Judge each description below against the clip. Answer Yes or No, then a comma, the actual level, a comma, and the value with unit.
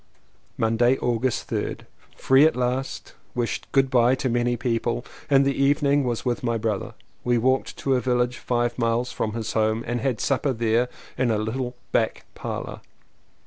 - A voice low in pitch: Yes, low, 120 Hz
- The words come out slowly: No, average, 170 wpm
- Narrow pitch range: Yes, narrow, 2.1 semitones